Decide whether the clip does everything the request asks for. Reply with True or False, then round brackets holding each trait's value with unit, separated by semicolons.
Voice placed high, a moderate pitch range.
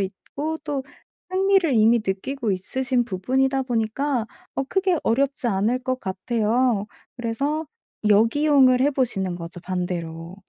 False (245 Hz; 5.9 semitones)